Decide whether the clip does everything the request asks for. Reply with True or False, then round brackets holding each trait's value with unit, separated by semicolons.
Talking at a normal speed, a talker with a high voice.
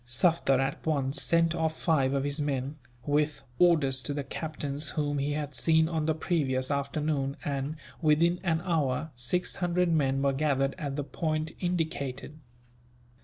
False (160 wpm; 150 Hz)